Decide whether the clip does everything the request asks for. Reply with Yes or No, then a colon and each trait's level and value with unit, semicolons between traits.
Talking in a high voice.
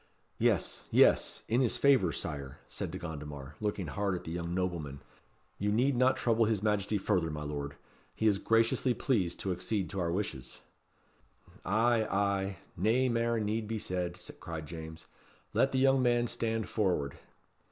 No: low, 100 Hz